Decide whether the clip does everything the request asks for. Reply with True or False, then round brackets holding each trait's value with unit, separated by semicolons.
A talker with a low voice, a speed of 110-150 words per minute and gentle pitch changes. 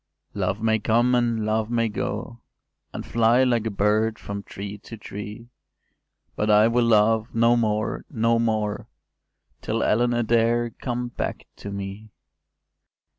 True (110 Hz; 145 wpm; 1.8 semitones)